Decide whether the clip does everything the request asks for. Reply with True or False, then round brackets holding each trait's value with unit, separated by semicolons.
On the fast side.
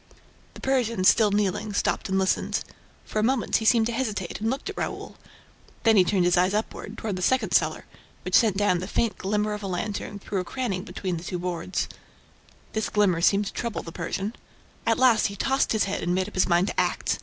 True (220 wpm)